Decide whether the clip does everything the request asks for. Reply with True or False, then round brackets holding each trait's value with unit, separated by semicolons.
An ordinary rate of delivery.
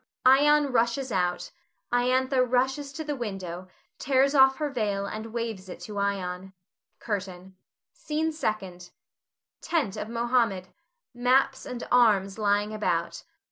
False (125 wpm)